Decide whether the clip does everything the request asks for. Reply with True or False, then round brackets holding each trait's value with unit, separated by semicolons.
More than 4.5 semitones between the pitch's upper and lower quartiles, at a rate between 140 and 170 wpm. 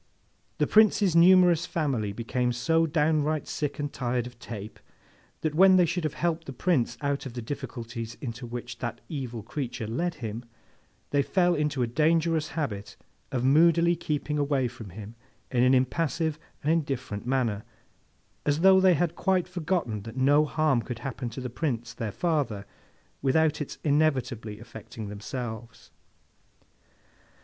True (5.2 semitones; 155 wpm)